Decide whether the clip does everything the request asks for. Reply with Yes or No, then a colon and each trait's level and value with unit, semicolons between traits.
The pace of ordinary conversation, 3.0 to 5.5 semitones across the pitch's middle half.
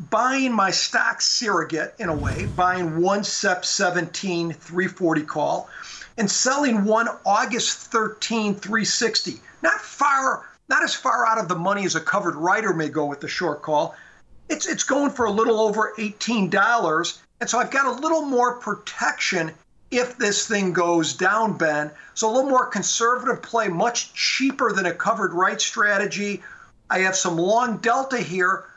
Yes: average, 165 wpm; average, 4.7 semitones